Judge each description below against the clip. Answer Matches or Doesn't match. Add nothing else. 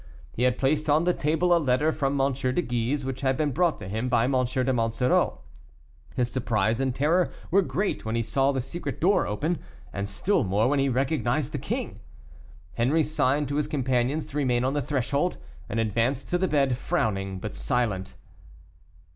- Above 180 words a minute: Matches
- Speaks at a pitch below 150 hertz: Matches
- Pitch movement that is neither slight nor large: Matches